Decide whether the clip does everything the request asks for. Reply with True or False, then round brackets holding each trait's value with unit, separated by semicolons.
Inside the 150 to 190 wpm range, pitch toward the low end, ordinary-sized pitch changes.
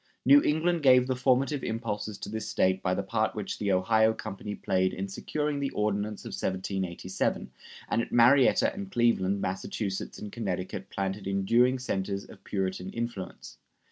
True (160 wpm; 105 Hz; 4.5 semitones)